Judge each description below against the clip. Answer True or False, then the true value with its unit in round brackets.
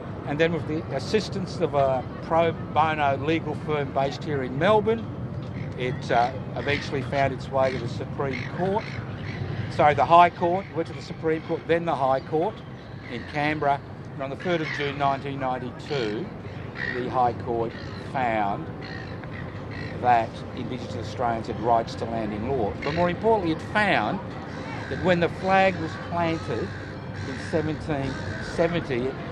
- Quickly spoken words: False (150 wpm)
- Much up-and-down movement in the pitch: False (4.5 semitones)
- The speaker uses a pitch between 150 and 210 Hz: False (140 Hz)